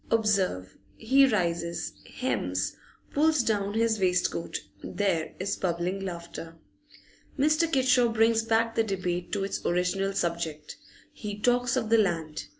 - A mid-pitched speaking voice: No, high, 200 Hz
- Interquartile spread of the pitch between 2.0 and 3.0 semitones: No, average, 4.7 semitones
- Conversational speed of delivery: No, slow, 130 wpm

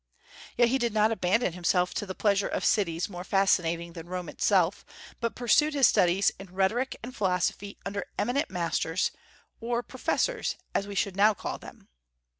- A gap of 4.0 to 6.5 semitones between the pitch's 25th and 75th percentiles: Yes, average, 4.3 semitones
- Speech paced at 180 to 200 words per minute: No, average, 170 wpm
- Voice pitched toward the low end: No, high, 195 Hz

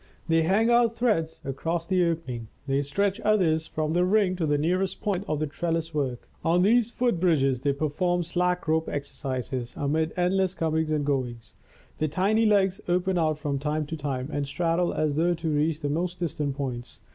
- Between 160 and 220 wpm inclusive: Yes, average, 190 wpm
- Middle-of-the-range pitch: Yes, medium, 160 Hz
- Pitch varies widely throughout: No, average, 3.8 semitones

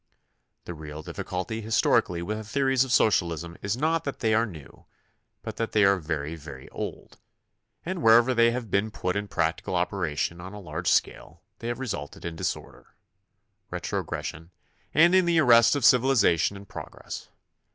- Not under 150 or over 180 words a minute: Yes, average, 175 wpm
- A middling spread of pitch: No, wide, 6.0 semitones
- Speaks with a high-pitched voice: No, low, 105 Hz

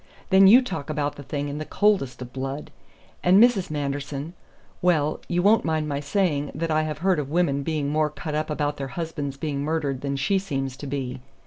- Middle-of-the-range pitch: Yes, medium, 150 Hz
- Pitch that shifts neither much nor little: Yes, average, 3.0 semitones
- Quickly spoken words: Yes, fast, 210 wpm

